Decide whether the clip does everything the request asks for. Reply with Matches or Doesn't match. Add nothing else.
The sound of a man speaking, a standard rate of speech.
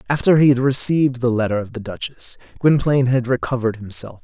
Matches